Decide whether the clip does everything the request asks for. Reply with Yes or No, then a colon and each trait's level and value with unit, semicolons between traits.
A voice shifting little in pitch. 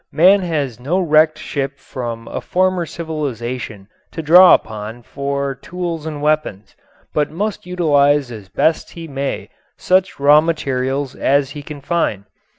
No: average, 3.9 semitones